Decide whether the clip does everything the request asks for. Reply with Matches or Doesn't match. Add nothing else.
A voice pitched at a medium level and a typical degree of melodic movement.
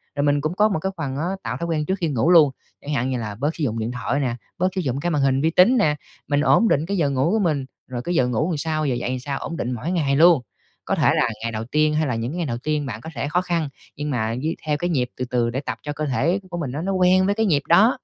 Matches